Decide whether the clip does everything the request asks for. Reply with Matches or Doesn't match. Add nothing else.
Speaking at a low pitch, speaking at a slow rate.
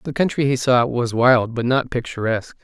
Doesn't match